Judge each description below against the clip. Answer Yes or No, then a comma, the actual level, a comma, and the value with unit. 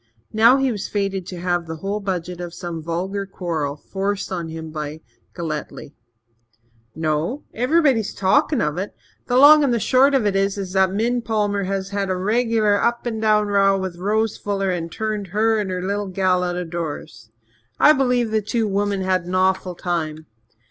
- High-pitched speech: Yes, high, 195 Hz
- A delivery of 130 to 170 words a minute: No, average, 185 wpm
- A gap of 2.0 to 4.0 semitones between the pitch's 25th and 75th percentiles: Yes, average, 3.6 semitones